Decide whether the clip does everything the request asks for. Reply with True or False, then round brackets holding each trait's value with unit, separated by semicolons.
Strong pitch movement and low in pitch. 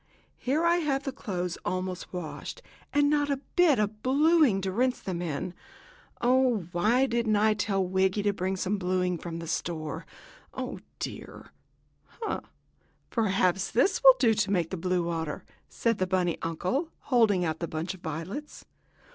False (6.1 semitones; 195 Hz)